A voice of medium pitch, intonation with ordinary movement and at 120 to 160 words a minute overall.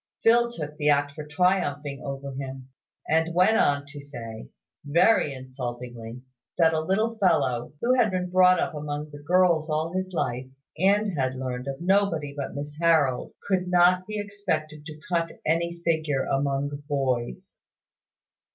Yes: medium, 155 Hz; average, 4.7 semitones; average, 155 wpm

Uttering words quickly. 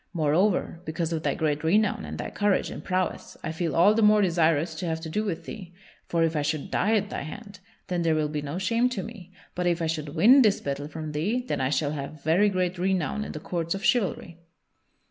Yes: fast, 240 wpm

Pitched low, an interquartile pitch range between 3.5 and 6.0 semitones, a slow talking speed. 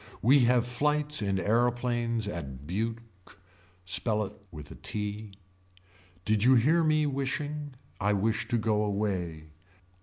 Yes: low, 110 Hz; average, 4.1 semitones; slow, 130 wpm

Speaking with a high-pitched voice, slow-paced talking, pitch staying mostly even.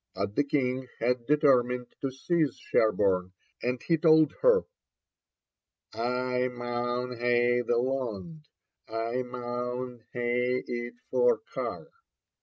No: low, 125 Hz; slow, 110 wpm; narrow, 1.9 semitones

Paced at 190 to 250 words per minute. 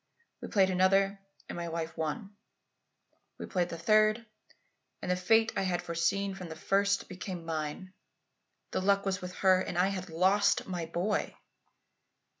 No: average, 160 wpm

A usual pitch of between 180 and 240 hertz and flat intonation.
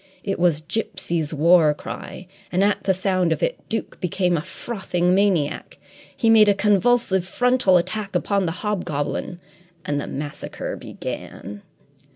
No: medium, 185 Hz; average, 3.7 semitones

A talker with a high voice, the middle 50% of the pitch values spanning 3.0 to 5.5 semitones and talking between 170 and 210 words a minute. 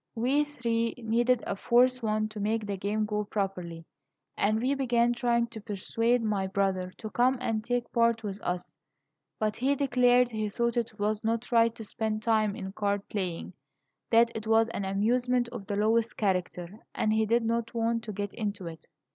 No: high, 220 Hz; narrow, 2.5 semitones; average, 190 wpm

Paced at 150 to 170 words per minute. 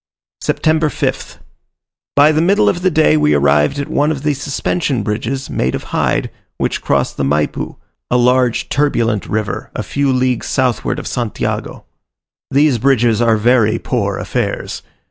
Yes: average, 155 wpm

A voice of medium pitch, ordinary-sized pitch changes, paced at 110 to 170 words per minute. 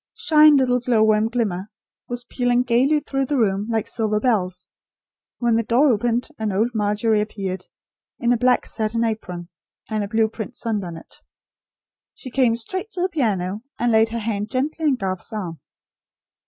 No: high, 225 Hz; average, 3.0 semitones; average, 165 wpm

